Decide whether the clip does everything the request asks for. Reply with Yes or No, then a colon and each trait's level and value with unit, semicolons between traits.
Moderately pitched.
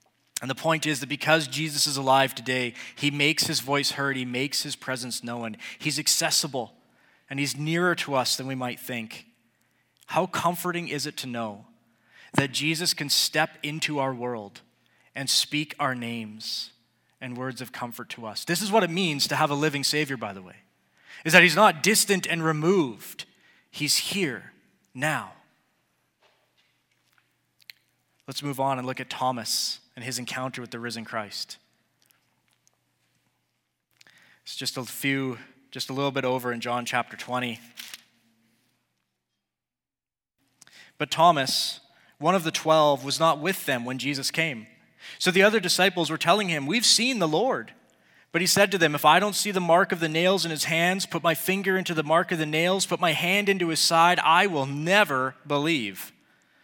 Yes: medium, 145 Hz